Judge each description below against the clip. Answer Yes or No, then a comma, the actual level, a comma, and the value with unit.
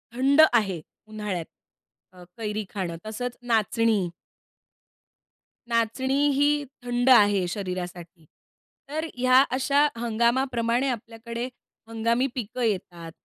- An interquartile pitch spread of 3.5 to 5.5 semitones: Yes, average, 3.8 semitones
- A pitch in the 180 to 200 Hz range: No, high, 230 Hz